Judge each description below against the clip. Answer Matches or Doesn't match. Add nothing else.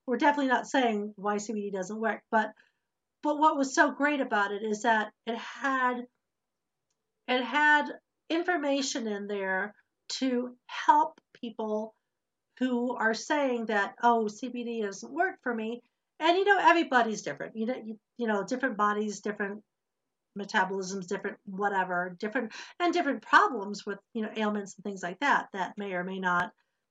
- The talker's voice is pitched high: Matches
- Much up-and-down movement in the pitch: Doesn't match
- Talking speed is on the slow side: Doesn't match